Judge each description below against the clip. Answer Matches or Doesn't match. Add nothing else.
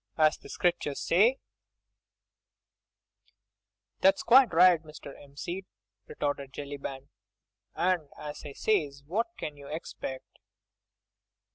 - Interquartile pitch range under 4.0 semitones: Doesn't match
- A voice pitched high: Doesn't match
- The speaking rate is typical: Doesn't match